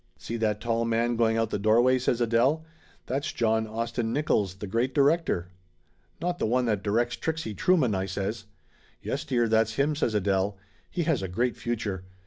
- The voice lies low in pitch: Yes, low, 115 Hz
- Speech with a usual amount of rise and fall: Yes, average, 3.2 semitones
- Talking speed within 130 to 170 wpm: No, average, 190 wpm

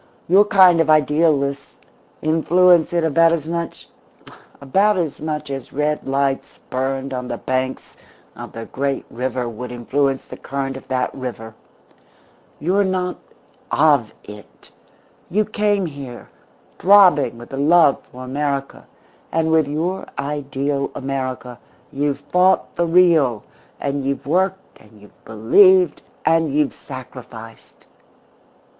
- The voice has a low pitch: No, medium, 145 Hz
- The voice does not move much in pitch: No, average, 4.3 semitones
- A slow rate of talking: Yes, slow, 125 wpm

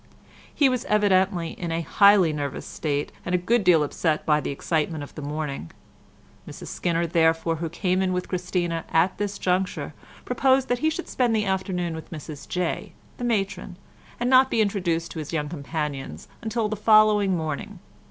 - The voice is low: No, medium, 180 Hz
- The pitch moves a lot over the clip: No, average, 4.4 semitones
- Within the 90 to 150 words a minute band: No, average, 180 wpm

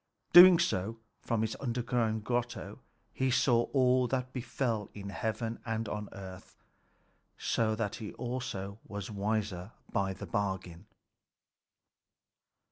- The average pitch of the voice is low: Yes, low, 110 Hz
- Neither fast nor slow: No, slow, 120 wpm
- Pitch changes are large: No, average, 3.3 semitones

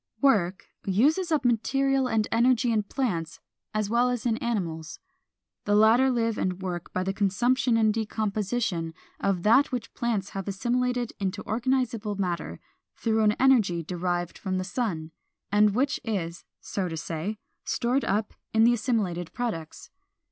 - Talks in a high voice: Yes, high, 215 Hz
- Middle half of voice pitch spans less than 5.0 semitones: Yes, average, 4.5 semitones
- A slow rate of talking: No, average, 155 wpm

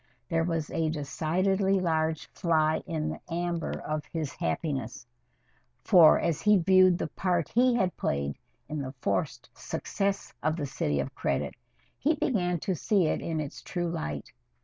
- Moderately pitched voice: Yes, medium, 165 Hz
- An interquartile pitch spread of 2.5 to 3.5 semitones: Yes, average, 3.2 semitones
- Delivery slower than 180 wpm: Yes, average, 160 wpm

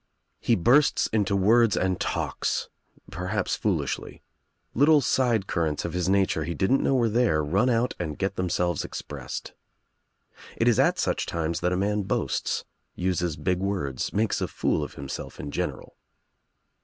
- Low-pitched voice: Yes, very low, 95 Hz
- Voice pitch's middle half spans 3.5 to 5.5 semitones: Yes, average, 4.6 semitones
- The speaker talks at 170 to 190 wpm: No, average, 155 wpm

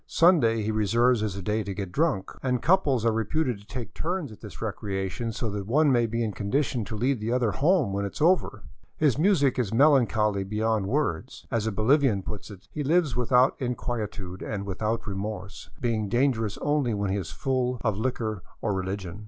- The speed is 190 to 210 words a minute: Yes, average, 200 wpm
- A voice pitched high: No, low, 115 Hz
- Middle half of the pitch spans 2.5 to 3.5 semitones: No, average, 4.5 semitones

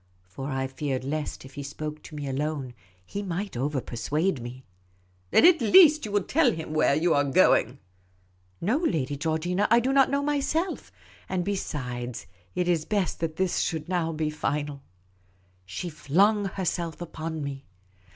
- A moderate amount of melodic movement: No, wide, 6.0 semitones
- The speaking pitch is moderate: Yes, medium, 155 Hz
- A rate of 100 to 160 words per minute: No, average, 175 wpm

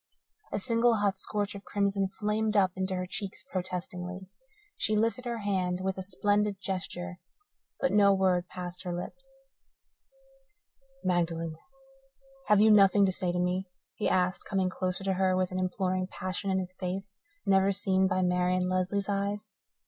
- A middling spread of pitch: No, narrow, 1.8 semitones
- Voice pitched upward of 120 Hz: Yes, high, 190 Hz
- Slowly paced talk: No, average, 160 wpm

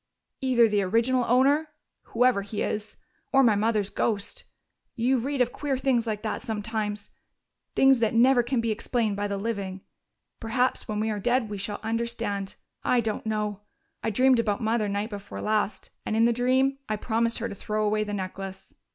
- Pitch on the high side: Yes, high, 225 Hz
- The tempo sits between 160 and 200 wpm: Yes, average, 185 wpm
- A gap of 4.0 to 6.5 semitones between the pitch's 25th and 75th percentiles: No, average, 2.8 semitones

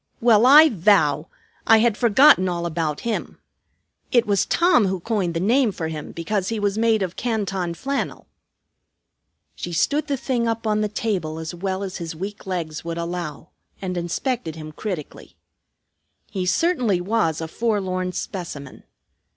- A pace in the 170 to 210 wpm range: No, average, 160 wpm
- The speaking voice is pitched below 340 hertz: Yes, high, 190 Hz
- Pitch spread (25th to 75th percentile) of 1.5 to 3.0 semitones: No, average, 5.0 semitones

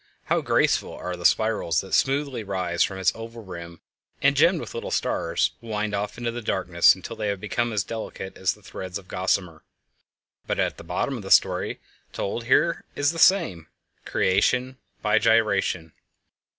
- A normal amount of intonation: Yes, average, 4.0 semitones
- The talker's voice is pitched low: Yes, low, 105 Hz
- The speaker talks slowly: No, average, 160 wpm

